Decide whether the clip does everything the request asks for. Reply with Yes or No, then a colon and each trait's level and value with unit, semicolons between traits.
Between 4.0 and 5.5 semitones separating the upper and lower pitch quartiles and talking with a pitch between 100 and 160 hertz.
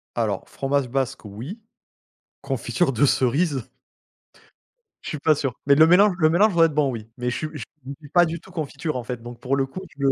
Yes: average, 4.7 semitones; medium, 140 Hz